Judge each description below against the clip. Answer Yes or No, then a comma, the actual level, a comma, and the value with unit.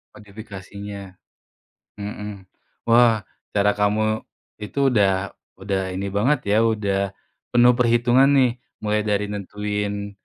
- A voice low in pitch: Yes, low, 105 Hz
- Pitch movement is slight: Yes, narrow, 2.2 semitones